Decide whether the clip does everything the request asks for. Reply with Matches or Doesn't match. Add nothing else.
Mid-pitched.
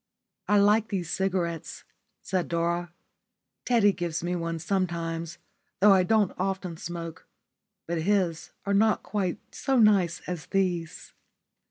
Matches